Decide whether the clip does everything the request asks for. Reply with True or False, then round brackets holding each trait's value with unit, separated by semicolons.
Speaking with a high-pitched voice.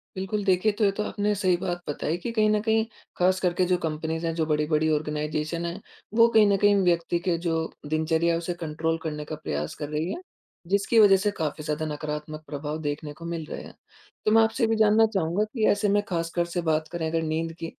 False (170 Hz)